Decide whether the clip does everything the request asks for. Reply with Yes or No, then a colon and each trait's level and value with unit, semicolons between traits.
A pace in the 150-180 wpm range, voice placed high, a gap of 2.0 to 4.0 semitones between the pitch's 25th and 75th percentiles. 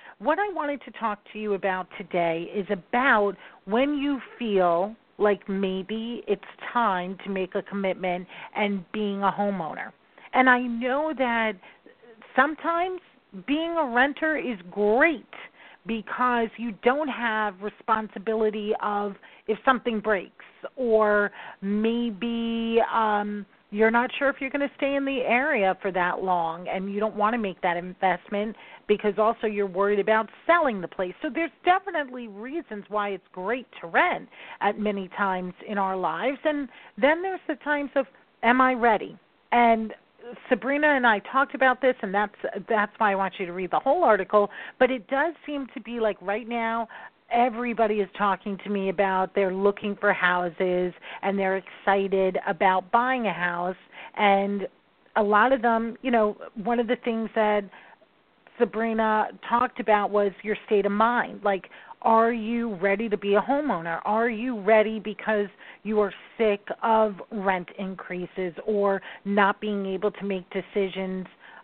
Yes: average, 160 wpm; high, 215 Hz; average, 3.5 semitones